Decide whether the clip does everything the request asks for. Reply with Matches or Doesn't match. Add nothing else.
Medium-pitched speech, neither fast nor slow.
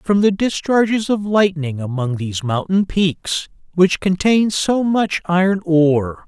Matches